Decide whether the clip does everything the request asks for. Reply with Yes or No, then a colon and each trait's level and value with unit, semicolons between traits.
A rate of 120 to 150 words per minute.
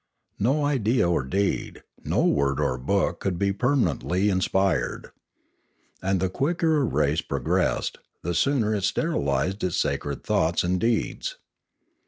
Yes: average, 140 wpm